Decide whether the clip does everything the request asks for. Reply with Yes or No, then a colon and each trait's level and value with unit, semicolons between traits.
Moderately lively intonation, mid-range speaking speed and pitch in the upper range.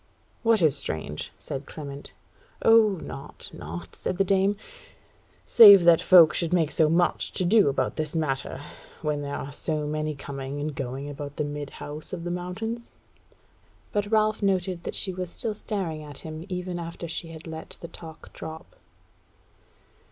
No: average, 4.1 semitones; average, 165 wpm; medium, 160 Hz